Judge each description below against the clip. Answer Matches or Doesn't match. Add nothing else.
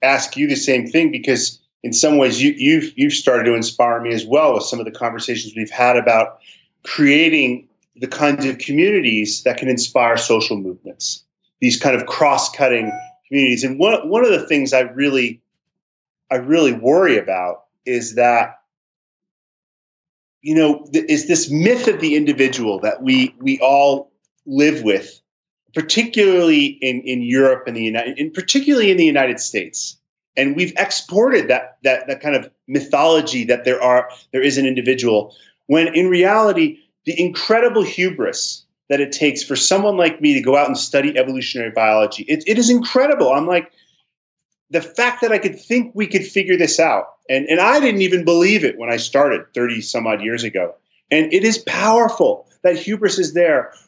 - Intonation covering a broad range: Matches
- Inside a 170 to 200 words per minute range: Matches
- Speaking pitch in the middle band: Matches